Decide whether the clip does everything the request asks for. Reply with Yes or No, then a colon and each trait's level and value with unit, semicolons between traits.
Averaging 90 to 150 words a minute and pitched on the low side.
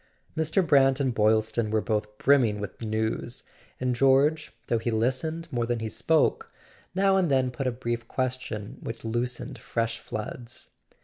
No: average, 160 wpm; low, 120 Hz